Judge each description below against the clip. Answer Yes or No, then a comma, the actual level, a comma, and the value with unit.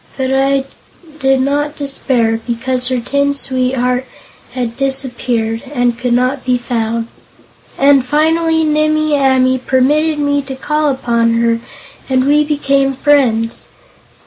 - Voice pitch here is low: No, very high, 265 Hz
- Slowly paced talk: Yes, slow, 125 wpm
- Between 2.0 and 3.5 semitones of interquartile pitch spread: Yes, narrow, 2.6 semitones